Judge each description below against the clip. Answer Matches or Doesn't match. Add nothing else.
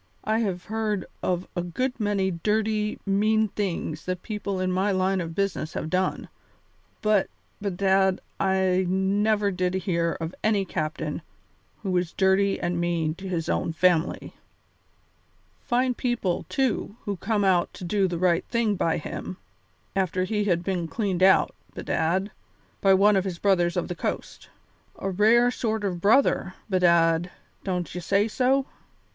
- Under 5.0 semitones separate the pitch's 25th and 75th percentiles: Matches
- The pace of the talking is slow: Doesn't match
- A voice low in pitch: Doesn't match